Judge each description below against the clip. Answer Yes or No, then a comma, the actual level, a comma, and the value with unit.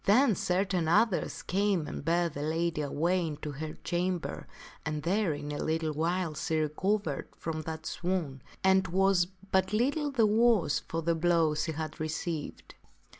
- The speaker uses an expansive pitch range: No, average, 3.4 semitones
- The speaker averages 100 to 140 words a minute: No, average, 165 wpm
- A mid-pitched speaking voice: Yes, medium, 170 Hz